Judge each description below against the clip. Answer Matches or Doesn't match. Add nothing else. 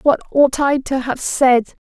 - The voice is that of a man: Doesn't match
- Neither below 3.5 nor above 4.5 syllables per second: Matches